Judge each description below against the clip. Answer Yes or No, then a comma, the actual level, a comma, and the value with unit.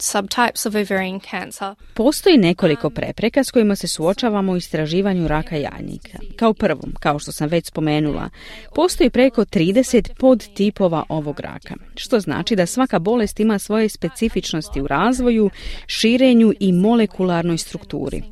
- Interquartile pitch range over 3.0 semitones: Yes, average, 5.0 semitones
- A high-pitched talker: Yes, high, 200 Hz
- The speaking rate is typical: Yes, average, 125 wpm